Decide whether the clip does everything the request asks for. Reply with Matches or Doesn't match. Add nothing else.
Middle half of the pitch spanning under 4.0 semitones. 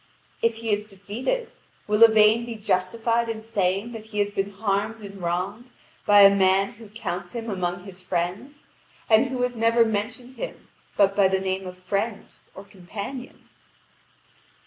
Matches